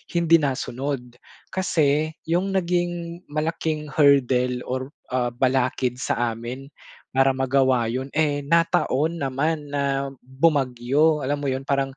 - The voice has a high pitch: No, medium, 140 Hz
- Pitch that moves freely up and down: No, average, 3.4 semitones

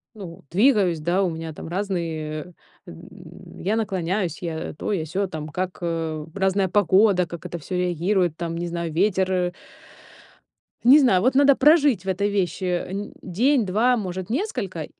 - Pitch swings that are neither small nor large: Yes, average, 3.3 semitones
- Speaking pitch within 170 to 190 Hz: Yes, medium, 185 Hz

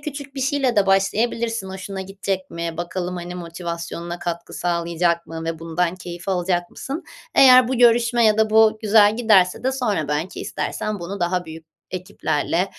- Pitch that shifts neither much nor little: Yes, average, 4.4 semitones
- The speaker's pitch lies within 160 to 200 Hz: Yes, medium, 185 Hz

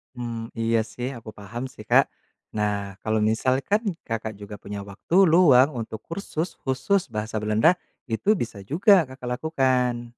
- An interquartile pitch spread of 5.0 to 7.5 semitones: Yes, wide, 5.4 semitones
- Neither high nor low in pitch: No, low, 120 Hz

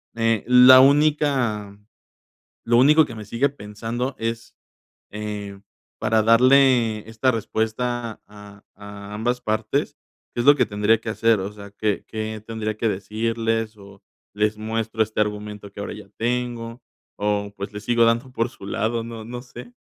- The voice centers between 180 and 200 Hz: No, low, 110 Hz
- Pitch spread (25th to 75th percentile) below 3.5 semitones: Yes, narrow, 2.4 semitones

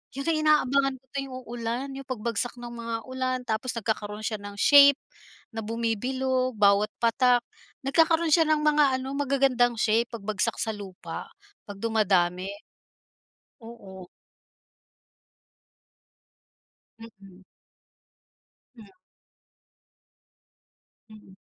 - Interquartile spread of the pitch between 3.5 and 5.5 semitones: Yes, average, 4.1 semitones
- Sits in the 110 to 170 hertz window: No, high, 235 Hz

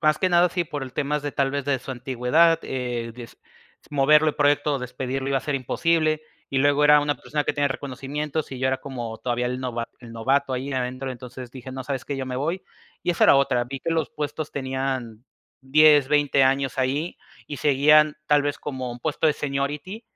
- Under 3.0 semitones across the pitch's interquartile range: Yes, narrow, 2.4 semitones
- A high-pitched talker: No, medium, 140 Hz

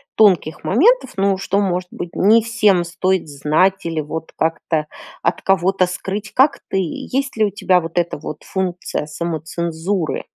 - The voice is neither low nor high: Yes, medium, 180 Hz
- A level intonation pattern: No, average, 3.3 semitones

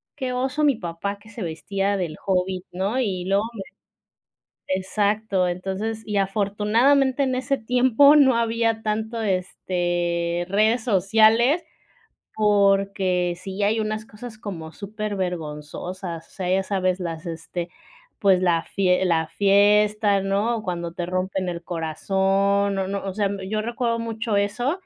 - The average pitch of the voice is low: No, high, 200 Hz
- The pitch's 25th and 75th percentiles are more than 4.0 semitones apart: No, average, 3.2 semitones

